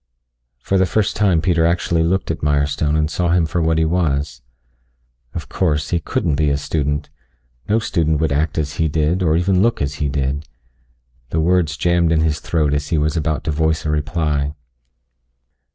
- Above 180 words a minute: Yes, average, 190 wpm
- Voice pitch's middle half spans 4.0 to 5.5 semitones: No, narrow, 2.6 semitones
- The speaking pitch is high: No, very low, 80 Hz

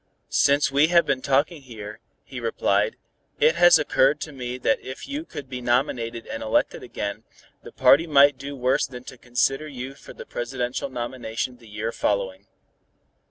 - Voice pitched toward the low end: Yes, low, 130 Hz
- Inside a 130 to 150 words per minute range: No, average, 170 wpm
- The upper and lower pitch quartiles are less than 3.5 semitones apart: Yes, average, 3.1 semitones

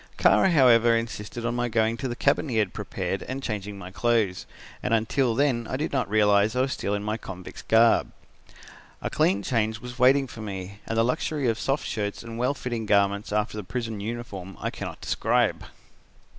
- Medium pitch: No, low, 115 Hz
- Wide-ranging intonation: No, average, 3.1 semitones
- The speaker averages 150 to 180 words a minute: No, average, 200 wpm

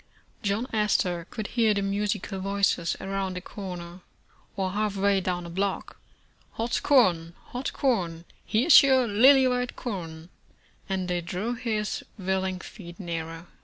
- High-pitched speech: Yes, high, 195 Hz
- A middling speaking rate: Yes, average, 150 wpm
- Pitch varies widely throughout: No, average, 3.5 semitones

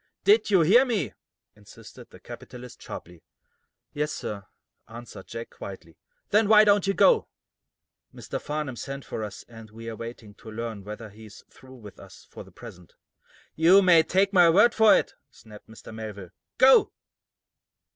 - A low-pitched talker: Yes, low, 120 Hz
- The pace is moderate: Yes, average, 165 wpm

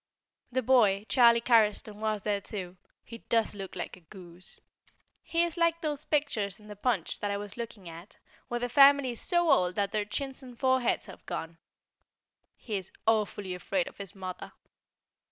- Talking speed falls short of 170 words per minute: No, average, 175 wpm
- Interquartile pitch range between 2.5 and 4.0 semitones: No, average, 4.6 semitones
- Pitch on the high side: Yes, high, 215 Hz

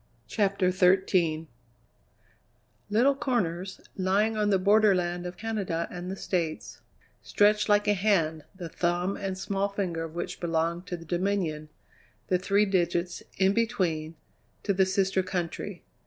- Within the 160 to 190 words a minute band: No, average, 140 wpm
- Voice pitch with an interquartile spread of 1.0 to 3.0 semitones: Yes, narrow, 2.6 semitones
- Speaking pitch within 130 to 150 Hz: No, medium, 185 Hz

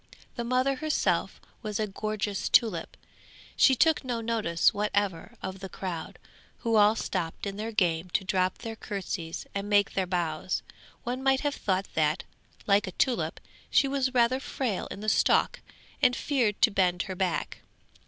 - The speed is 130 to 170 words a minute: Yes, average, 165 wpm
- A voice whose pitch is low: No, high, 205 Hz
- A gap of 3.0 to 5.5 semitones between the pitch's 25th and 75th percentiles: Yes, average, 4.3 semitones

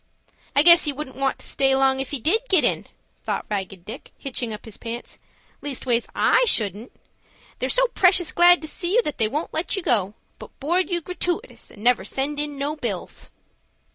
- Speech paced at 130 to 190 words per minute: No, average, 200 wpm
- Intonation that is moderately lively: No, wide, 6.4 semitones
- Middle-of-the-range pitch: No, very high, 280 Hz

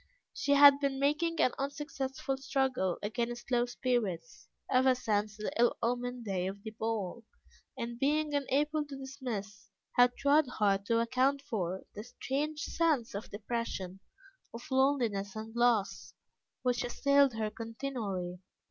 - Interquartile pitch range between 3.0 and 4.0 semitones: No, average, 4.5 semitones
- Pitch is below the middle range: No, high, 245 Hz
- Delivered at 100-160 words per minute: Yes, average, 140 wpm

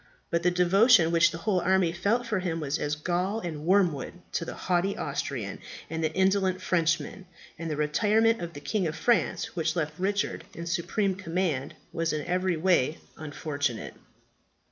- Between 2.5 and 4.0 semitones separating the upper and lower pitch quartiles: Yes, average, 3.0 semitones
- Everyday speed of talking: Yes, average, 170 wpm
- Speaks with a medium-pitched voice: Yes, medium, 175 Hz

